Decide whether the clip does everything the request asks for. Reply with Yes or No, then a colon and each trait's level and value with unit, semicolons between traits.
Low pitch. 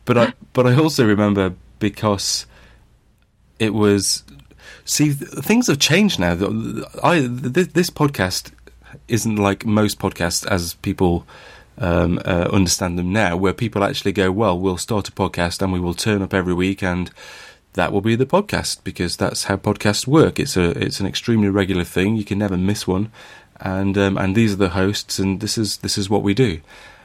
Yes: low, 100 Hz